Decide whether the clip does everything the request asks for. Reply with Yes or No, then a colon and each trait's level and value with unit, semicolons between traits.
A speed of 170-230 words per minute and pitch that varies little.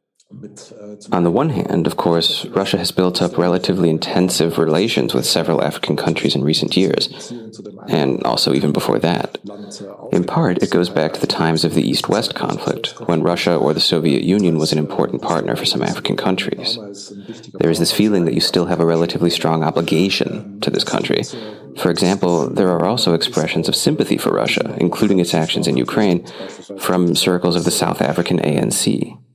Yes: average, 180 wpm; narrow, 2.1 semitones